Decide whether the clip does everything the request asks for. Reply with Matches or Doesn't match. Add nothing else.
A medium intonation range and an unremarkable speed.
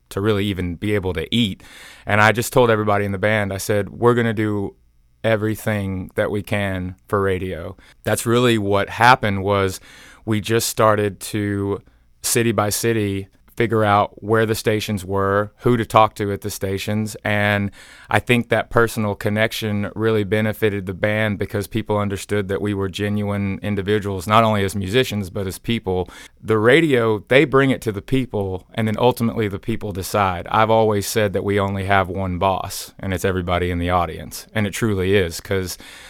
Doesn't match